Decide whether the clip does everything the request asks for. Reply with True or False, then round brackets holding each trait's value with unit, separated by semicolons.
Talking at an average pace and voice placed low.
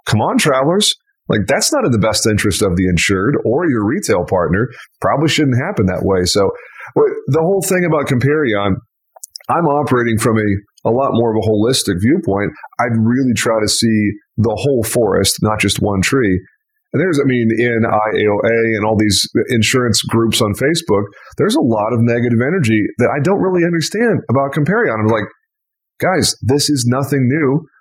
True (180 wpm; 120 Hz)